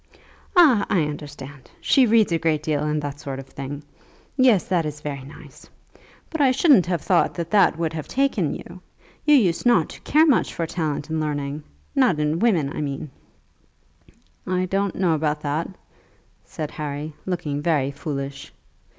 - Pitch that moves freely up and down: No, average, 4.8 semitones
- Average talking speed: Yes, average, 170 wpm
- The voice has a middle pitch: Yes, medium, 160 Hz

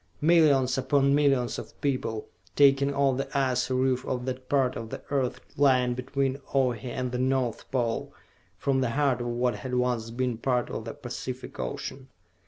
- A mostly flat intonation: Yes, narrow, 1.8 semitones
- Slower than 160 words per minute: No, average, 175 wpm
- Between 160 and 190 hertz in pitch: No, low, 130 Hz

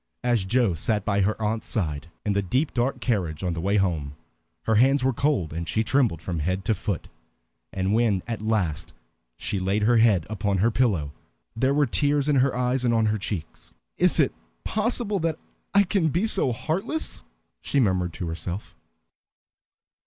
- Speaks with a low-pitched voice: Yes, low, 110 Hz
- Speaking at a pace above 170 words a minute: Yes, average, 180 wpm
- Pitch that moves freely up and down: Yes, wide, 5.8 semitones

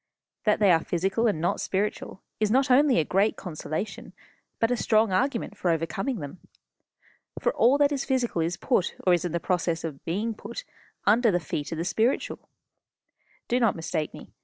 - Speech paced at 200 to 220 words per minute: No, average, 185 wpm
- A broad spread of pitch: Yes, wide, 5.8 semitones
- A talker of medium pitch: No, high, 200 Hz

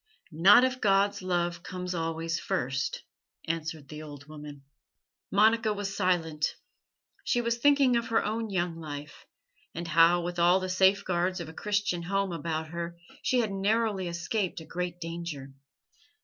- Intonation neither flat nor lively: Yes, average, 3.5 semitones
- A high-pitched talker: No, medium, 175 Hz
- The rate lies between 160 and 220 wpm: No, average, 150 wpm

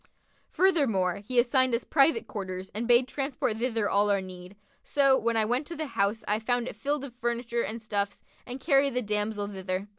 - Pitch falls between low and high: No, high, 235 Hz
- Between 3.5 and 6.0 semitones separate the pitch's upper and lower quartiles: Yes, average, 4.2 semitones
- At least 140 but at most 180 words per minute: No, fast, 205 wpm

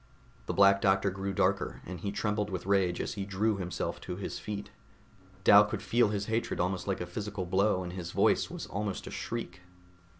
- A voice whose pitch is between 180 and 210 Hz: No, low, 100 Hz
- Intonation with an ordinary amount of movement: No, narrow, 2.1 semitones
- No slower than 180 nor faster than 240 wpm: Yes, average, 200 wpm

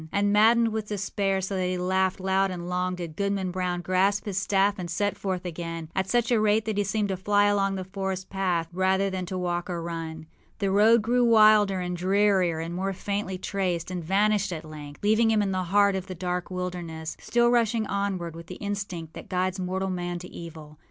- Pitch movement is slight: Yes, narrow, 2.3 semitones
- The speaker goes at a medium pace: No, fast, 220 wpm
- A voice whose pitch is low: No, high, 190 Hz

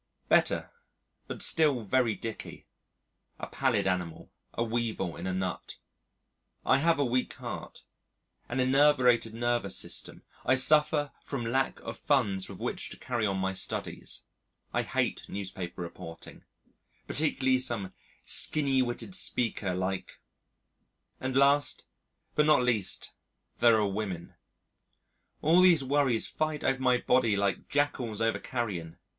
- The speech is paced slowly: Yes, slow, 130 wpm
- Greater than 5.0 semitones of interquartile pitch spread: Yes, wide, 5.4 semitones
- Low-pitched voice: Yes, low, 120 Hz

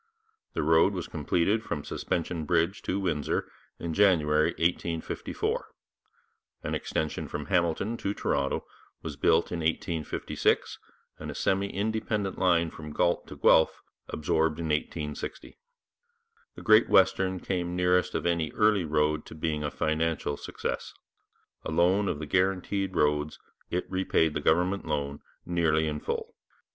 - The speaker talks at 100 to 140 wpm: Yes, slow, 135 wpm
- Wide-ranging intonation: No, average, 3.3 semitones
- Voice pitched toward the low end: Yes, very low, 85 Hz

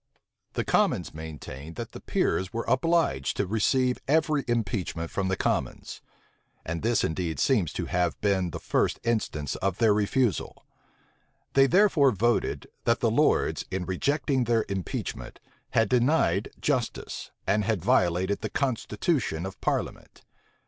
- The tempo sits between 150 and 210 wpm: No, average, 140 wpm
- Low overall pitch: Yes, low, 105 Hz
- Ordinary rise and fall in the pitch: No, wide, 6.1 semitones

